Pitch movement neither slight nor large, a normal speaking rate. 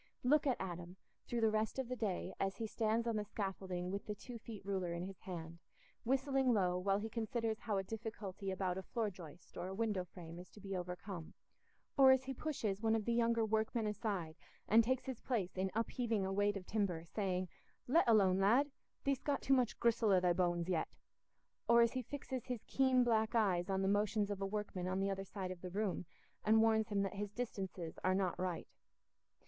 No: average, 3.7 semitones; fast, 215 wpm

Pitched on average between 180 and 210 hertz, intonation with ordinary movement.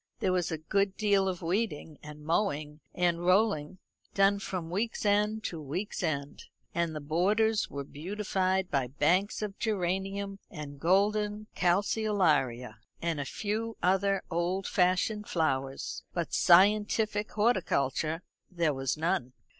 Yes: medium, 185 Hz; average, 4.6 semitones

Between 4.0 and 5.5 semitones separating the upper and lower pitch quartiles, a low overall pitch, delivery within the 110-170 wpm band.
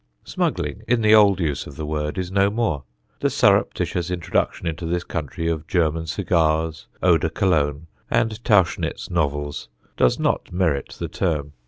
No: average, 3.5 semitones; very low, 85 Hz; average, 160 wpm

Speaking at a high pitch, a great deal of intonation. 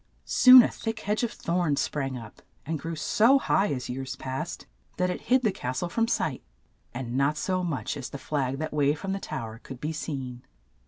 No: medium, 150 Hz; wide, 6.4 semitones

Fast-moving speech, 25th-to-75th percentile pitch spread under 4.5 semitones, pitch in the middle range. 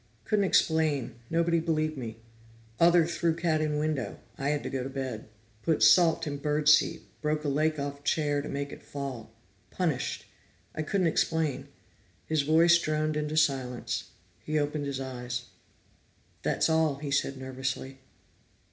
No: average, 150 wpm; average, 2.7 semitones; medium, 150 Hz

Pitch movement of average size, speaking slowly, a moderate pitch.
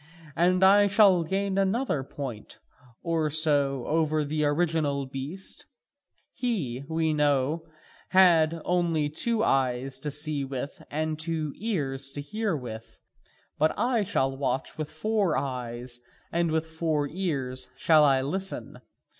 Yes: average, 4.4 semitones; slow, 130 wpm; medium, 155 Hz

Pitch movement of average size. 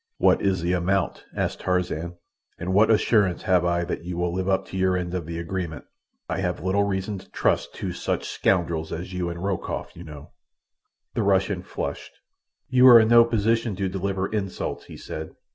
No: narrow, 2.2 semitones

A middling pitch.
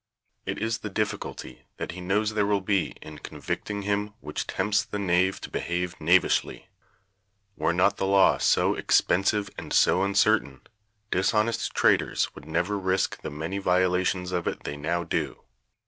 No: very low, 95 Hz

